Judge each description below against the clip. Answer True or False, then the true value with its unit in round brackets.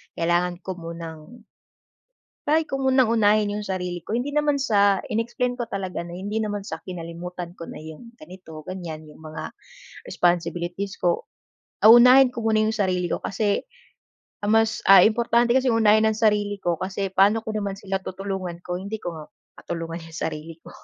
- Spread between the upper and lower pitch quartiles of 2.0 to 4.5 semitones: True (4.2 semitones)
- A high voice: True (195 Hz)